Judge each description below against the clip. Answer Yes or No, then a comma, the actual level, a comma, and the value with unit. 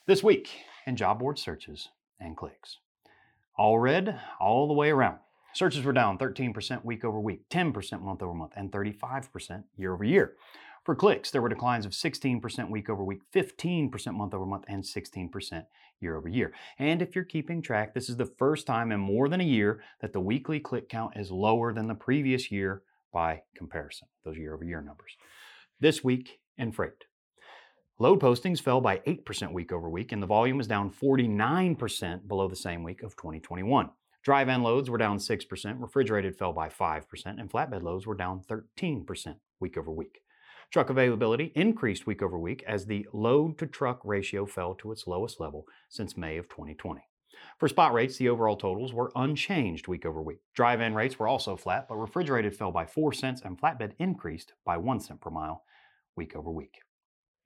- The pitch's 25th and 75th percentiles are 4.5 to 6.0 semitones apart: Yes, wide, 5.6 semitones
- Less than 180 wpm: No, average, 185 wpm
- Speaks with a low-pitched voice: Yes, low, 110 Hz